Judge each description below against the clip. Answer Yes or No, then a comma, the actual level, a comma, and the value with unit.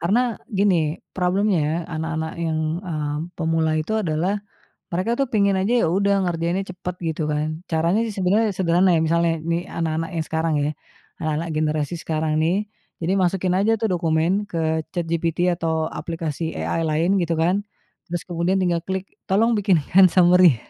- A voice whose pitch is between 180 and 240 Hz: No, medium, 170 Hz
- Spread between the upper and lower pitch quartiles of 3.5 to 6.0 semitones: No, average, 3.0 semitones